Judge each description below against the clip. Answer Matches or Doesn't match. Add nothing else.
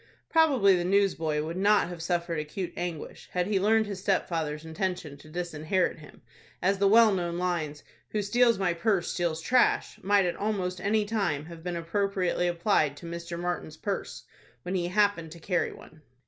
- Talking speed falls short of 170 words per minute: Doesn't match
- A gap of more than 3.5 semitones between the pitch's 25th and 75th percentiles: Doesn't match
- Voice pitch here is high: Doesn't match